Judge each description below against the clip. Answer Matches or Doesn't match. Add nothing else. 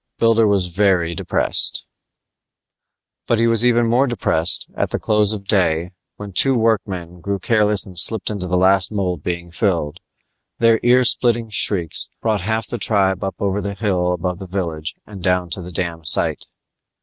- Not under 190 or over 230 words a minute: Doesn't match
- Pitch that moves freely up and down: Doesn't match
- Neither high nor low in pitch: Doesn't match